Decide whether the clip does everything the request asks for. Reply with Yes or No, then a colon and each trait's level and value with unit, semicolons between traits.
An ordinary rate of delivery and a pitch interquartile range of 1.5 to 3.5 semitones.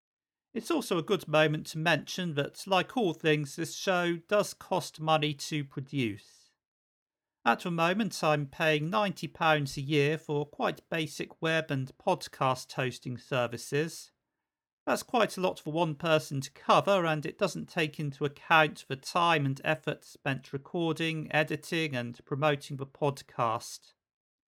Yes: average, 145 wpm; average, 2.8 semitones